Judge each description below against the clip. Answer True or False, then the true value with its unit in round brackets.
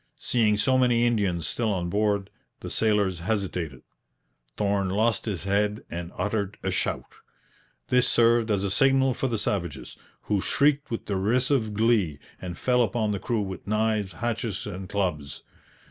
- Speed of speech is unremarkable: True (155 wpm)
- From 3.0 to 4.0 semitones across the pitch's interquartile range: True (3.5 semitones)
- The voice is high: False (105 Hz)